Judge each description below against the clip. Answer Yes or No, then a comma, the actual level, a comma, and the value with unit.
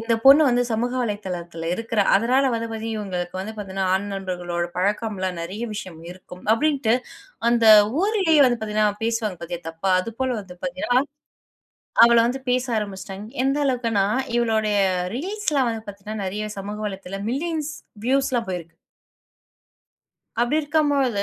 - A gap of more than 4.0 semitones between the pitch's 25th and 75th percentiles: Yes, average, 4.5 semitones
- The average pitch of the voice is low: No, high, 220 Hz